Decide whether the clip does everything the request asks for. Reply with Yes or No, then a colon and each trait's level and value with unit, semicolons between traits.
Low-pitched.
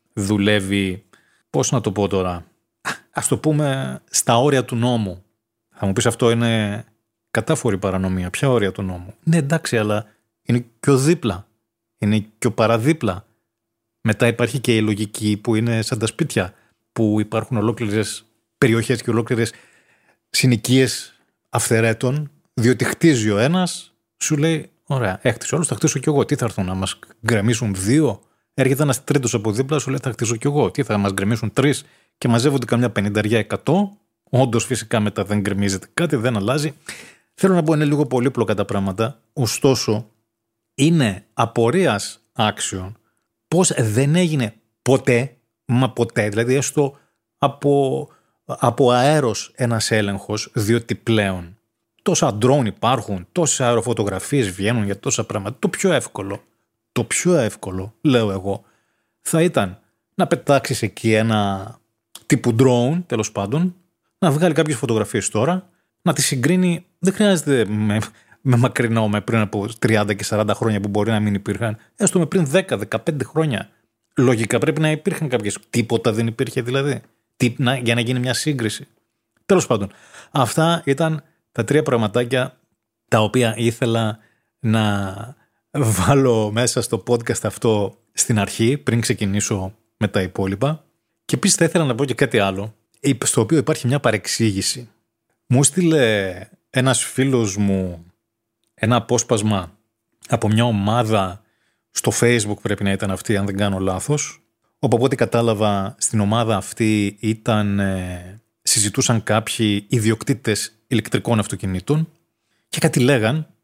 Yes: low, 115 Hz